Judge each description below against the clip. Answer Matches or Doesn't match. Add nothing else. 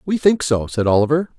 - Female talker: Doesn't match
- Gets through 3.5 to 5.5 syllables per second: Doesn't match